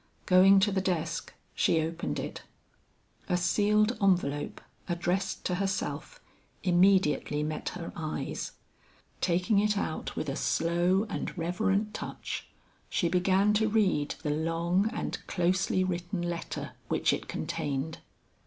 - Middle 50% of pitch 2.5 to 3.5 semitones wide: Yes, average, 2.8 semitones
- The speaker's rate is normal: No, slow, 125 wpm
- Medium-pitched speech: Yes, medium, 180 Hz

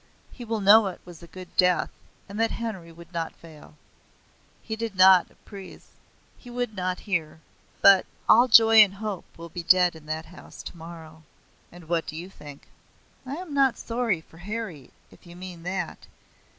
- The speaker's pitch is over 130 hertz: Yes, medium, 185 Hz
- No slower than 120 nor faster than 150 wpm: No, average, 180 wpm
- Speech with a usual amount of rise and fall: Yes, average, 4.6 semitones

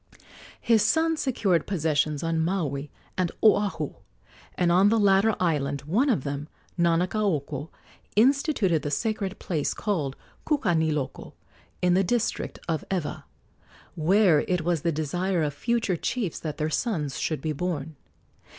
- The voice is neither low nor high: Yes, medium, 175 Hz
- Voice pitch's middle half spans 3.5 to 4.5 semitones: No, average, 5.1 semitones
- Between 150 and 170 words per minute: No, slow, 135 wpm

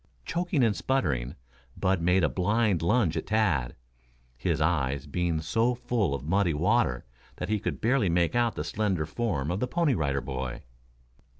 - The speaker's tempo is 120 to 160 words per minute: No, average, 170 wpm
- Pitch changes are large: Yes, wide, 7.1 semitones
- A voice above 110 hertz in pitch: No, very low, 90 Hz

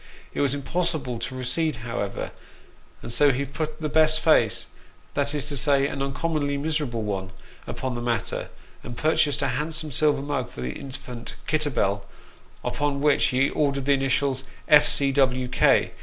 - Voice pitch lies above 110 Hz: Yes, medium, 140 Hz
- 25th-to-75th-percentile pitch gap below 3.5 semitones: Yes, average, 3.0 semitones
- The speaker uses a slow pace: No, average, 170 wpm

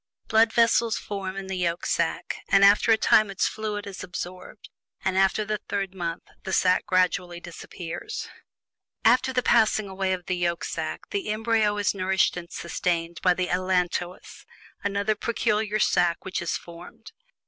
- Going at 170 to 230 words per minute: No, average, 160 wpm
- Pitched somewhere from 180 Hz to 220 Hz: Yes, high, 190 Hz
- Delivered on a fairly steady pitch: No, average, 3.1 semitones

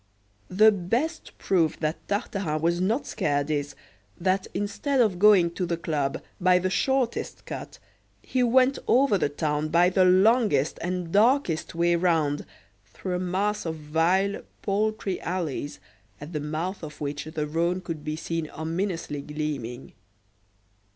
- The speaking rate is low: No, average, 145 wpm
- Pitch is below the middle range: No, medium, 175 Hz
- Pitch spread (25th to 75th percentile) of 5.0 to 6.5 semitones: No, average, 4.4 semitones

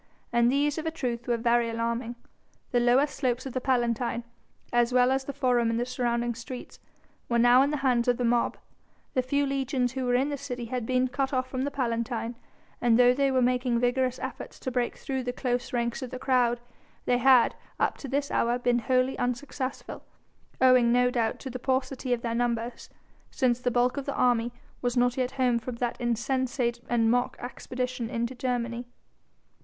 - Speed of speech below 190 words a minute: No, average, 200 wpm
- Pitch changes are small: Yes, narrow, 1.4 semitones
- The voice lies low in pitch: No, high, 245 Hz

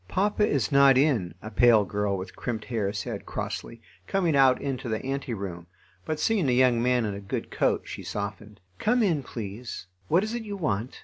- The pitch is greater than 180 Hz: No, low, 125 Hz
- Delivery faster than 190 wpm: Yes, average, 200 wpm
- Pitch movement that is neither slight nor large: No, wide, 6.0 semitones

